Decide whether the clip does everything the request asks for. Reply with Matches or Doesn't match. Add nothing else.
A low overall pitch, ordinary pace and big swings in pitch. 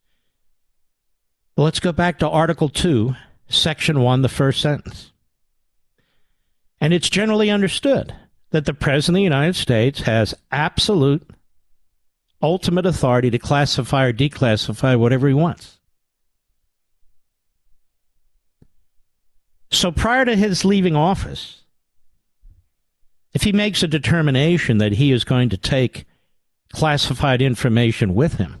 Doesn't match